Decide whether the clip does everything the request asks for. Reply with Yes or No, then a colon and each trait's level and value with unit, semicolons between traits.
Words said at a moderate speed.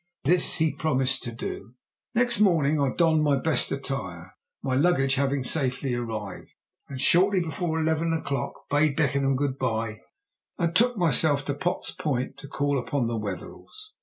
Yes: average, 160 wpm